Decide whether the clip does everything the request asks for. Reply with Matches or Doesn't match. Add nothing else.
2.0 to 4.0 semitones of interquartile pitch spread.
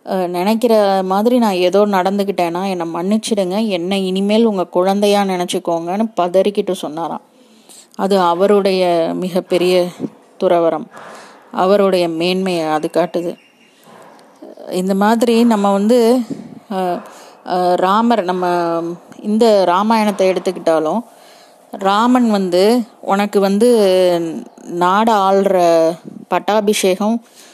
Matches